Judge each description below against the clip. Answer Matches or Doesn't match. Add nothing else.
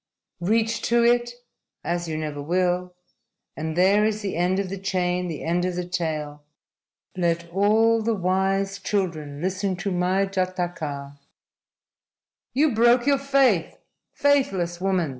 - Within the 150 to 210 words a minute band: Doesn't match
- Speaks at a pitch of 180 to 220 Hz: Matches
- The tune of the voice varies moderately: Matches